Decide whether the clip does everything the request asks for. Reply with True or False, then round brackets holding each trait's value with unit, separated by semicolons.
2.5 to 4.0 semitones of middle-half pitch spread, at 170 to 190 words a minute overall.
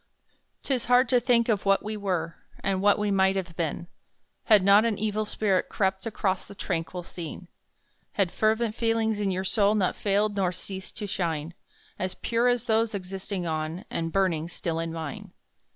True (3.3 semitones; 180 wpm)